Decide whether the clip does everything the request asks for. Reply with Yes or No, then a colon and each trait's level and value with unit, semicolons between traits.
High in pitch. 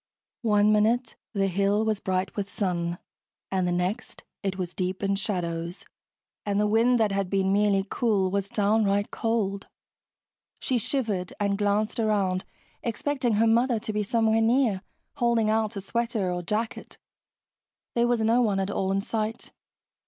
Yes: high, 205 Hz